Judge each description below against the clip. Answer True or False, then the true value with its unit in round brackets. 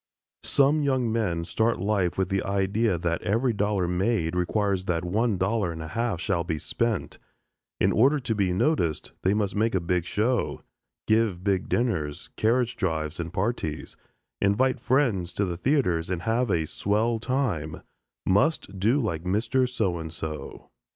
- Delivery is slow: False (165 wpm)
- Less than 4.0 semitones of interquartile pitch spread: False (4.9 semitones)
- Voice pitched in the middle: False (100 Hz)